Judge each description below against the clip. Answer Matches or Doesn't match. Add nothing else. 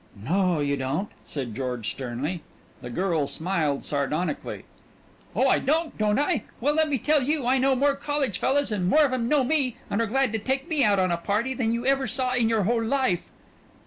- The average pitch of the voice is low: Doesn't match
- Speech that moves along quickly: Matches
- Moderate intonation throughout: Doesn't match